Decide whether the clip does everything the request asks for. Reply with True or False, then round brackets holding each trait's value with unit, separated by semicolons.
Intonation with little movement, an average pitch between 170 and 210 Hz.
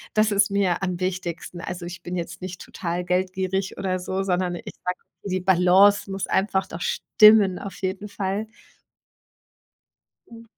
True (1.6 semitones; 185 Hz)